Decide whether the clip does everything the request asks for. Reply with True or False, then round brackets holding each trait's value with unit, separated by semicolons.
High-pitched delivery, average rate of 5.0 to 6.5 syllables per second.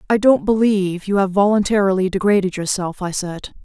True (195 Hz; 5.6 syllables/s)